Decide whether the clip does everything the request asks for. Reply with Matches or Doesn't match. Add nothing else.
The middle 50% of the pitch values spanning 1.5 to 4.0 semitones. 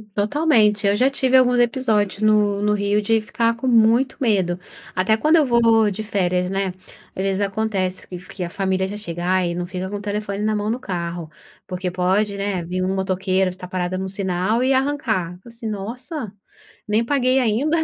Matches